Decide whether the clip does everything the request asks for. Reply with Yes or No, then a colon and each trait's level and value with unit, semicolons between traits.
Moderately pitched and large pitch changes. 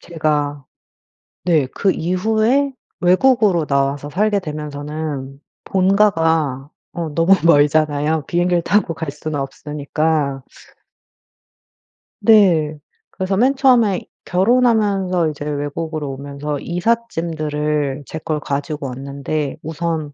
No: medium, 155 Hz; average, 4.3 semitones